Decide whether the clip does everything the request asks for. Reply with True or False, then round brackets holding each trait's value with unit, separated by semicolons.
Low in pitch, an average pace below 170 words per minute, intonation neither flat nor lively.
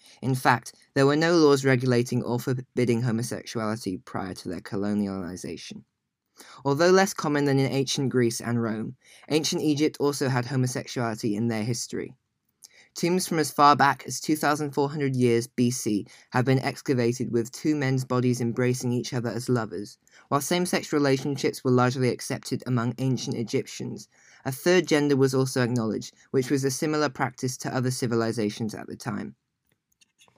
True (130 Hz; 155 wpm; 3.0 semitones)